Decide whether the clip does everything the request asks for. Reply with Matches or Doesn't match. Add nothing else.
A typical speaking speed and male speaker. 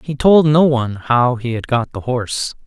Doesn't match